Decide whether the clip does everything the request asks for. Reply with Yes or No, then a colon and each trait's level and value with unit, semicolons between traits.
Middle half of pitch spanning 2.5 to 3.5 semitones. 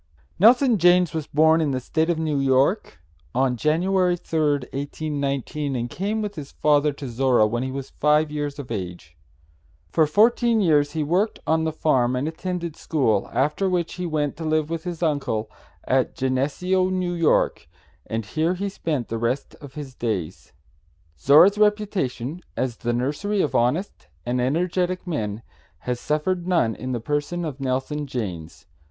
No: average, 5.2 semitones